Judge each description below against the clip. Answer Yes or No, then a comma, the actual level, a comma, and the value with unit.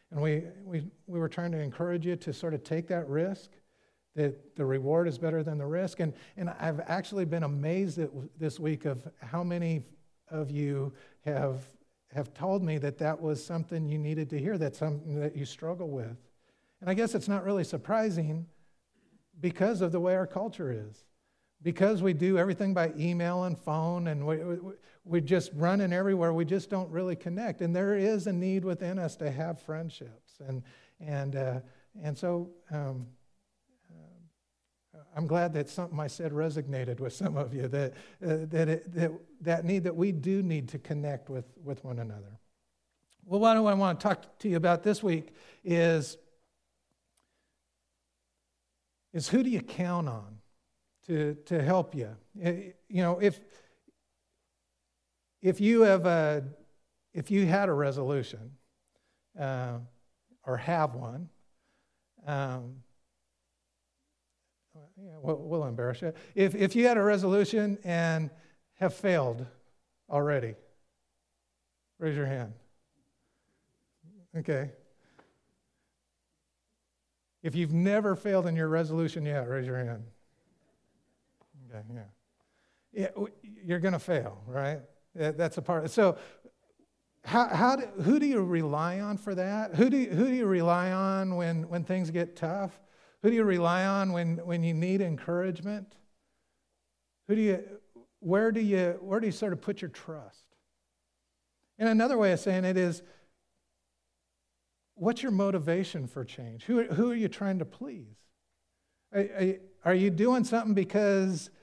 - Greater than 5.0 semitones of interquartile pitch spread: Yes, wide, 5.6 semitones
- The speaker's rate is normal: Yes, average, 155 wpm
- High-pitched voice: No, medium, 165 Hz